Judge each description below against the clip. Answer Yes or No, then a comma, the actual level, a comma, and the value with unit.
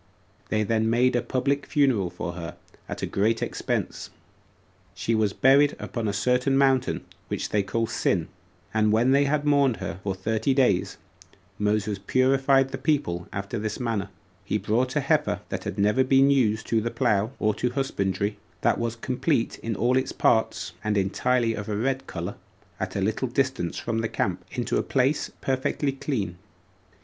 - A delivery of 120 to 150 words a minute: No, average, 175 wpm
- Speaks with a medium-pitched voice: No, low, 115 Hz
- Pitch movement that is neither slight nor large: Yes, average, 4.3 semitones